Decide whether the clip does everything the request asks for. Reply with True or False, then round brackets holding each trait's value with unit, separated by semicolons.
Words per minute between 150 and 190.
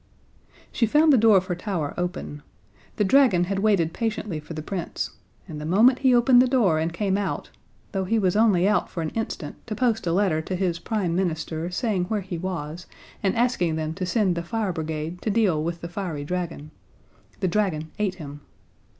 False (200 wpm)